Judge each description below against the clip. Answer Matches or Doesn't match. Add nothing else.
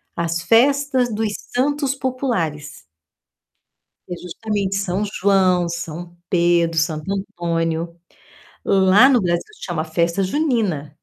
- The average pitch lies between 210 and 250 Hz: Doesn't match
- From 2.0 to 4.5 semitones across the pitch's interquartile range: Doesn't match